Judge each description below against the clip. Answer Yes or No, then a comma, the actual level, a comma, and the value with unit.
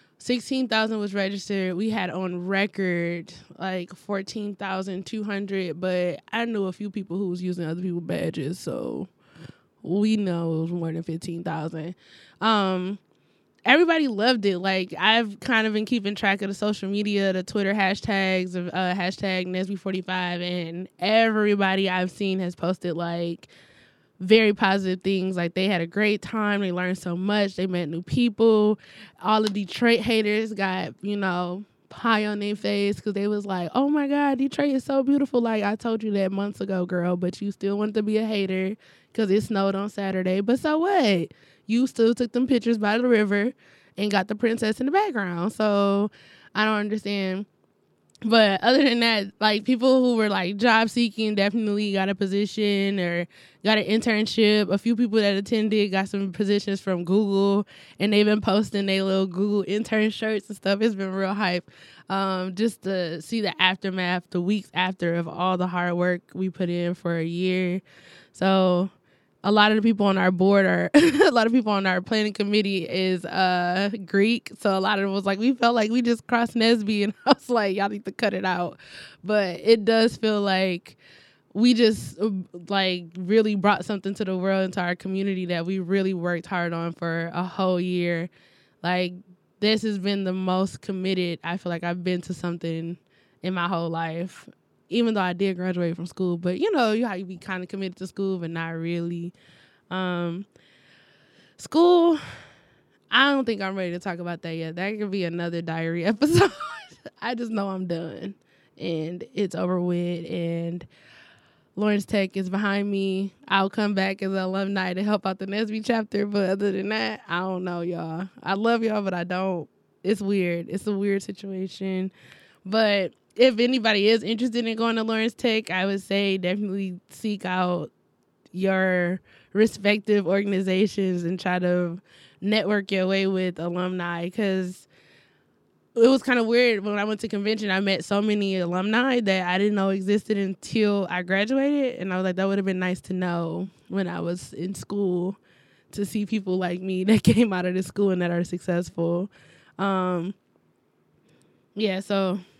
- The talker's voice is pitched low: No, high, 195 Hz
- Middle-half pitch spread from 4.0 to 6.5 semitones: No, average, 2.8 semitones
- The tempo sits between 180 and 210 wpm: Yes, average, 185 wpm